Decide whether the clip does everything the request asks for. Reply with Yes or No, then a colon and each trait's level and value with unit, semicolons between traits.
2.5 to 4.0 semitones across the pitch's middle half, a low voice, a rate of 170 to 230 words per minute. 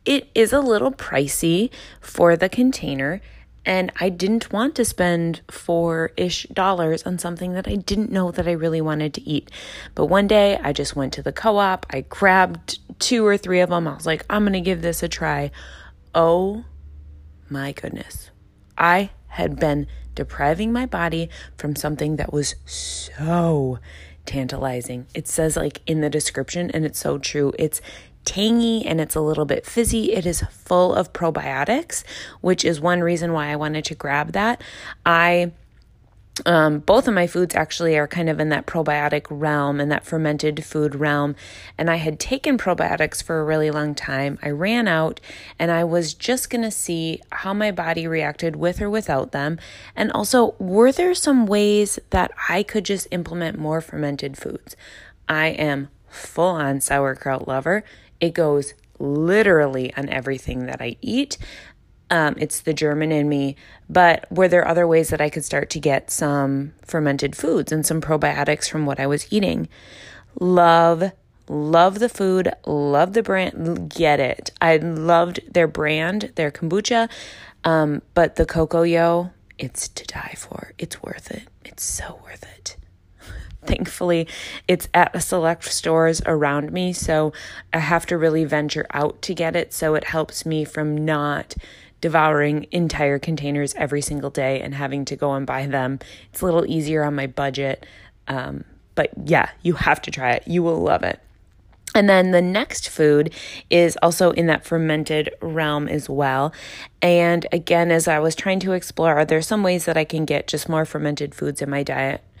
No: average, 3.4 semitones; medium, 160 Hz; average, 175 wpm